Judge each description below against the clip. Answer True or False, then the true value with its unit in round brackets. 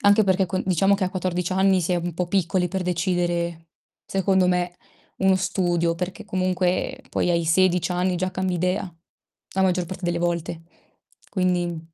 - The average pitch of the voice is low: False (180 Hz)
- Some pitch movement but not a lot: False (1.4 semitones)